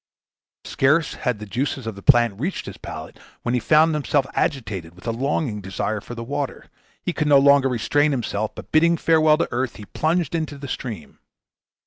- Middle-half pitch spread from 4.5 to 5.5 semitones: Yes, average, 5.2 semitones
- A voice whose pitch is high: No, low, 135 Hz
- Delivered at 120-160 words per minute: No, average, 190 wpm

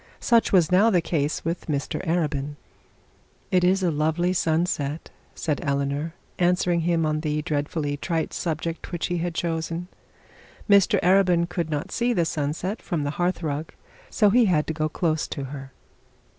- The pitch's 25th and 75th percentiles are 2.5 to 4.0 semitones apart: Yes, average, 2.8 semitones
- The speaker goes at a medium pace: Yes, average, 165 wpm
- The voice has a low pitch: No, medium, 165 Hz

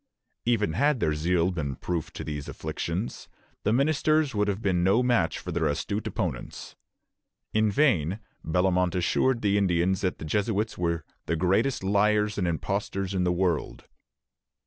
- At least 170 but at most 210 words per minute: No, average, 160 wpm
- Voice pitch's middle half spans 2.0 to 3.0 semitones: No, average, 3.8 semitones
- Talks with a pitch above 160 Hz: No, very low, 95 Hz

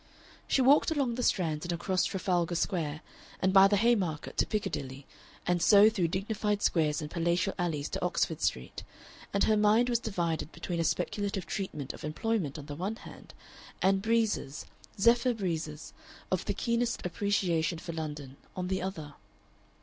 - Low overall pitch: No, medium, 185 Hz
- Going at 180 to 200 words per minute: No, average, 165 wpm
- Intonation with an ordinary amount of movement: Yes, average, 4.6 semitones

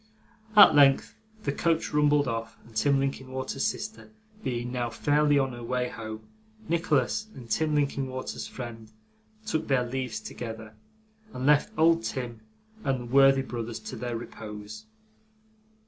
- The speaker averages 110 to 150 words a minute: Yes, average, 140 wpm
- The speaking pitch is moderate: No, low, 130 Hz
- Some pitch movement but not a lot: Yes, average, 3.6 semitones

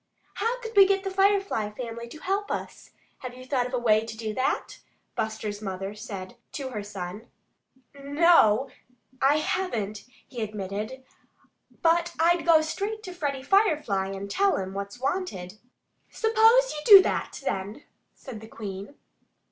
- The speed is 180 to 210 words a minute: No, average, 155 wpm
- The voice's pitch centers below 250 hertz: No, very high, 255 Hz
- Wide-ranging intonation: Yes, wide, 8.9 semitones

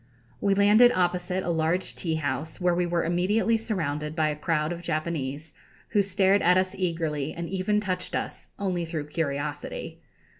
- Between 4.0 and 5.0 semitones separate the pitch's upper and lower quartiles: No, average, 3.3 semitones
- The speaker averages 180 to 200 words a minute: No, average, 160 wpm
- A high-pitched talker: No, medium, 175 Hz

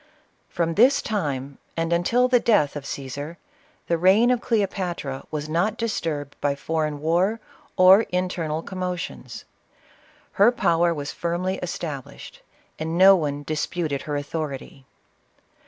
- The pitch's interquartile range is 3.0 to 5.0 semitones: Yes, average, 4.4 semitones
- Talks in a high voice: No, medium, 170 Hz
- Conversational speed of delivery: No, slow, 130 wpm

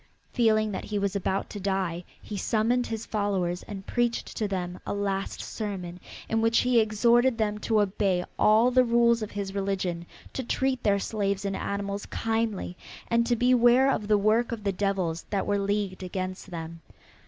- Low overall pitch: No, high, 205 Hz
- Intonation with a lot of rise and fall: No, average, 3.0 semitones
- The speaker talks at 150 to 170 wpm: No, average, 180 wpm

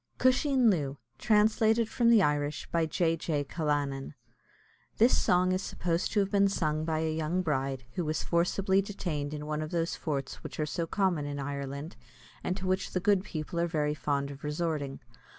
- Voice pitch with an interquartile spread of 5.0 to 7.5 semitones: No, average, 4.2 semitones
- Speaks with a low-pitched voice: No, medium, 160 Hz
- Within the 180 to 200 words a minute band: Yes, average, 185 wpm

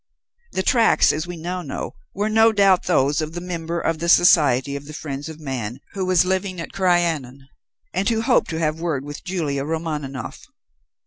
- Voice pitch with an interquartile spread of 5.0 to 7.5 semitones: No, average, 3.9 semitones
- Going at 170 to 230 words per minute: Yes, average, 190 wpm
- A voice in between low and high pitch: Yes, medium, 165 Hz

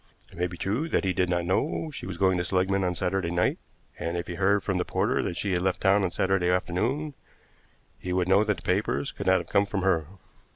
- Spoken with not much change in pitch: Yes, narrow, 1.9 semitones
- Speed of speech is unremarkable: No, fast, 250 wpm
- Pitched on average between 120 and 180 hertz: No, very low, 95 Hz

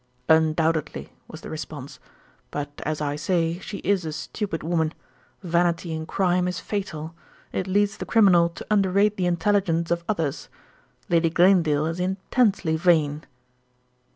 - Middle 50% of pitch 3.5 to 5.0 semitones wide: No, average, 3.1 semitones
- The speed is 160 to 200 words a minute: No, average, 140 wpm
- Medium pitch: Yes, medium, 170 Hz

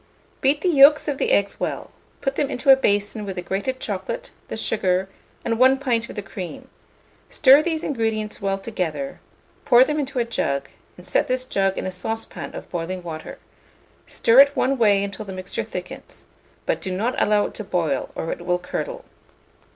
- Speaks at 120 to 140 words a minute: No, average, 190 wpm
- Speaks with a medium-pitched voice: No, high, 215 Hz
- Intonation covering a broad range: Yes, wide, 6.1 semitones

